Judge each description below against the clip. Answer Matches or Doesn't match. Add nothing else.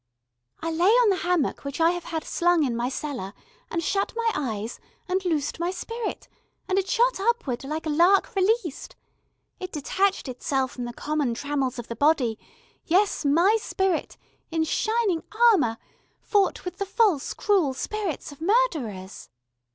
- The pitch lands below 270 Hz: Doesn't match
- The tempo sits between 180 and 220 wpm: Doesn't match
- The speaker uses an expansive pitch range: Matches